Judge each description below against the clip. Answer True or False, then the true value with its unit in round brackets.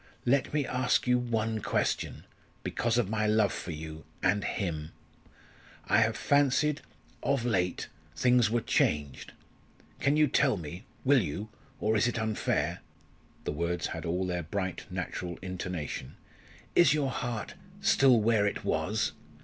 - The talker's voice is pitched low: True (110 Hz)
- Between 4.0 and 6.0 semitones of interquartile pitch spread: True (5.6 semitones)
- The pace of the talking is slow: False (145 wpm)